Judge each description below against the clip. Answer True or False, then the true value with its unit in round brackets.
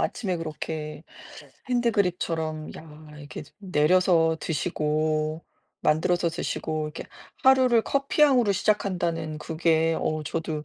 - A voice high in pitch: False (165 Hz)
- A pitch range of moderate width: True (3.3 semitones)